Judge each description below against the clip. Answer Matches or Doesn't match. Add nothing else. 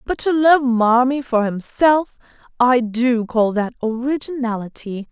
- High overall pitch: Matches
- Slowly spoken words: Matches